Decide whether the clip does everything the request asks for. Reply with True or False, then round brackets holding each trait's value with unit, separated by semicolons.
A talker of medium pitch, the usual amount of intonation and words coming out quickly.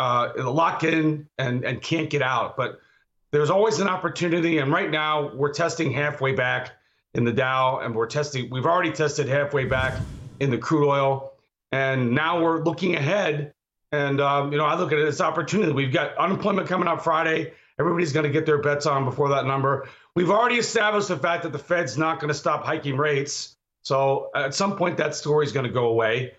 True (150 Hz; 3.5 semitones; 210 wpm)